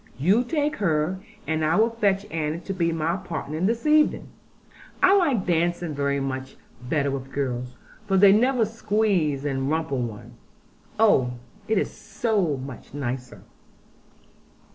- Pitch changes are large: Yes, wide, 7.1 semitones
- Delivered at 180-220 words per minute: No, average, 140 wpm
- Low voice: No, medium, 165 Hz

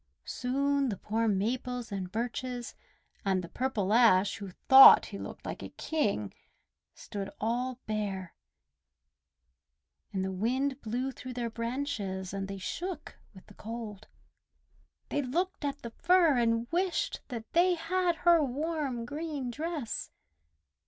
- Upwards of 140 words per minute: No, slow, 135 wpm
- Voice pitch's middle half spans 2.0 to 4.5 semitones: No, average, 5.3 semitones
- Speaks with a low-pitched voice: No, high, 245 Hz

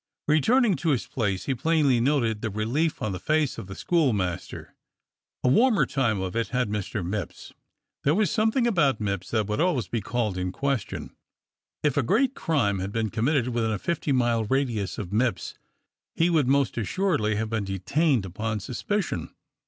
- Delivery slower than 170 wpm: No, average, 175 wpm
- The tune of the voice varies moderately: No, wide, 6.3 semitones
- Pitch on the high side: No, low, 120 Hz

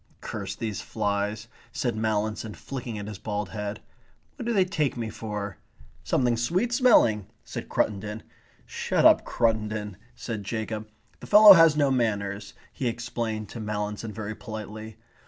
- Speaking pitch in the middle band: No, low, 110 Hz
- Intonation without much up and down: Yes, narrow, 2.3 semitones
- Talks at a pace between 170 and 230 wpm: No, average, 145 wpm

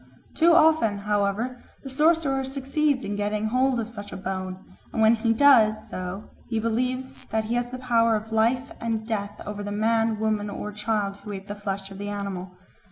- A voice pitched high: Yes, high, 220 Hz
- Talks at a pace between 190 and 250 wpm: Yes, average, 195 wpm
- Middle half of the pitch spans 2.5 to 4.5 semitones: Yes, average, 3.5 semitones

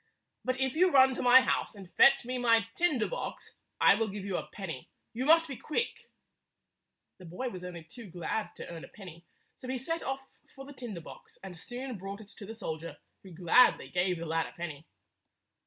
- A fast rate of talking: Yes, fast, 210 wpm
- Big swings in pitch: Yes, wide, 6.6 semitones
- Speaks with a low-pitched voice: No, high, 215 Hz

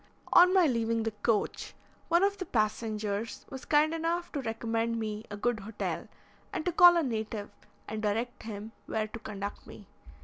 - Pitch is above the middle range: Yes, high, 225 Hz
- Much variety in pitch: Yes, wide, 6.0 semitones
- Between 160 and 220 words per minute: Yes, average, 175 wpm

